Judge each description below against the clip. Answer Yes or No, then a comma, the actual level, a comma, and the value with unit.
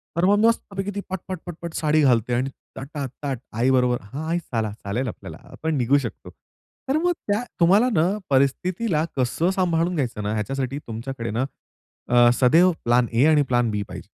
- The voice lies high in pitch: No, medium, 140 Hz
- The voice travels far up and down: Yes, wide, 6.1 semitones